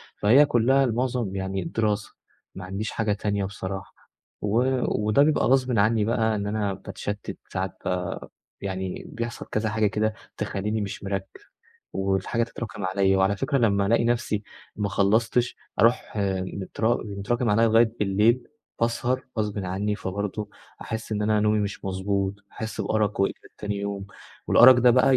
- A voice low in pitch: Yes, low, 105 Hz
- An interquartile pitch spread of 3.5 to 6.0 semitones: No, average, 2.8 semitones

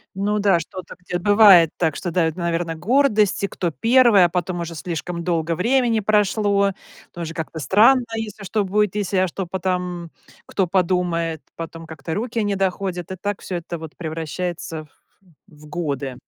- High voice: No, medium, 180 Hz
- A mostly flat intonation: No, average, 3.5 semitones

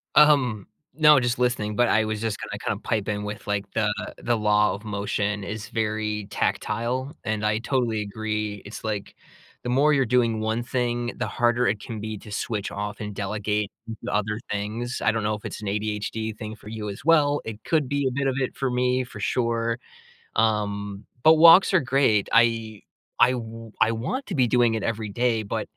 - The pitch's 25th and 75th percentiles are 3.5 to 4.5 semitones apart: No, narrow, 2.6 semitones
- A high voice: No, low, 110 Hz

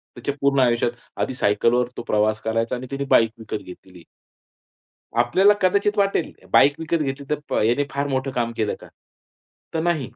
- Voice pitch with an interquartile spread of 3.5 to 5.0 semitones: Yes, average, 4.4 semitones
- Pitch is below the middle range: Yes, low, 130 Hz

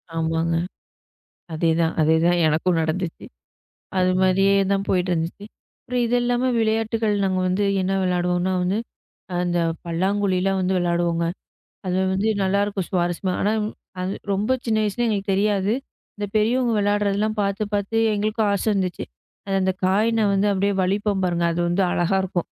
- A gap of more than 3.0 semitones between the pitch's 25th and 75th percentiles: No, average, 2.7 semitones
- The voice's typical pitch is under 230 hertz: Yes, high, 190 Hz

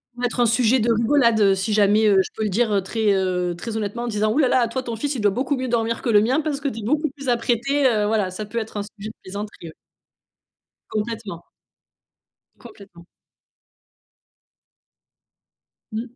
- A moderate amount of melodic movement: Yes, average, 3.0 semitones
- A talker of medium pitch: No, high, 225 Hz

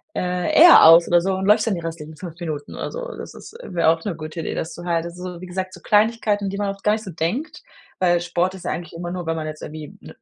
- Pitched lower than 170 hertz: No, medium, 175 Hz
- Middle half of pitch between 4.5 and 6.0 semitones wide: No, average, 2.8 semitones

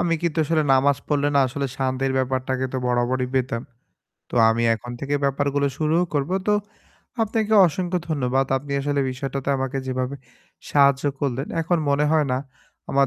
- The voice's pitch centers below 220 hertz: Yes, medium, 140 Hz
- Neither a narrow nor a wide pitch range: No, narrow, 2.2 semitones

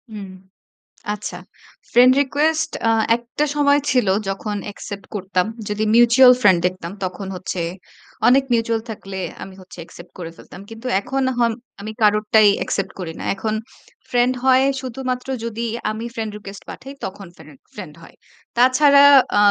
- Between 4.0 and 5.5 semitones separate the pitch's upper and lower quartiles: Yes, average, 4.8 semitones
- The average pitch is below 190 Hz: No, high, 220 Hz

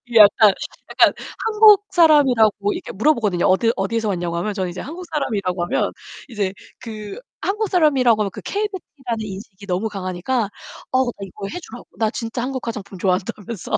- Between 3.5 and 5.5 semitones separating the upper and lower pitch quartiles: Yes, average, 5.2 semitones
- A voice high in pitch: Yes, high, 220 Hz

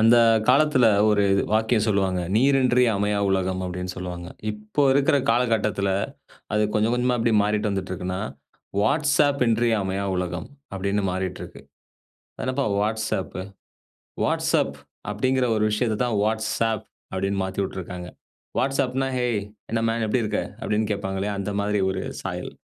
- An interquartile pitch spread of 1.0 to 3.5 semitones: No, average, 3.9 semitones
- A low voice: Yes, low, 105 Hz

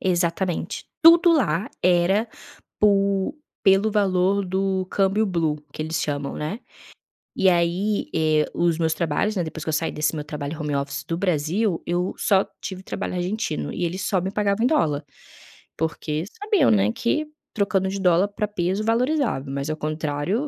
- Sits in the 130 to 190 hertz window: Yes, medium, 185 Hz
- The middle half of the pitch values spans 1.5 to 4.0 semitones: No, average, 4.5 semitones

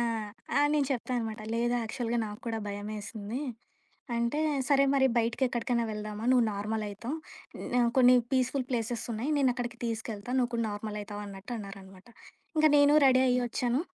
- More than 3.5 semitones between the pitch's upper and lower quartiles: No, average, 2.9 semitones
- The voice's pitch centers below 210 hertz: No, high, 235 Hz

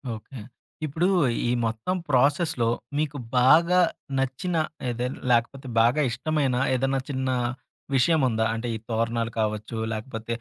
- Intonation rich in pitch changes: No, average, 3.9 semitones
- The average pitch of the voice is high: No, low, 125 Hz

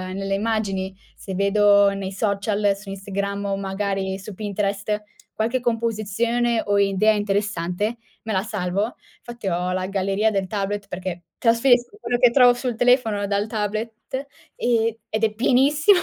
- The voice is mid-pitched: No, high, 205 Hz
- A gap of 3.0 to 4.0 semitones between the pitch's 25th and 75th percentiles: No, narrow, 2.6 semitones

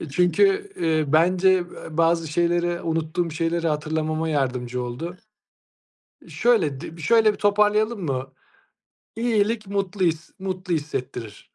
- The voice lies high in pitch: No, medium, 170 Hz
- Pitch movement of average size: Yes, average, 3.9 semitones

